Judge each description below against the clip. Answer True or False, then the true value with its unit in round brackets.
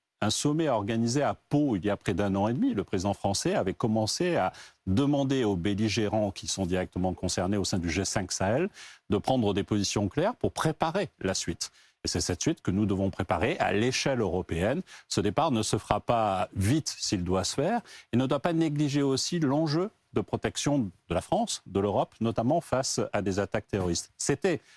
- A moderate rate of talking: True (200 wpm)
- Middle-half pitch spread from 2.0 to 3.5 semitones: False (4.9 semitones)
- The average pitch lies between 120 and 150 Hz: False (105 Hz)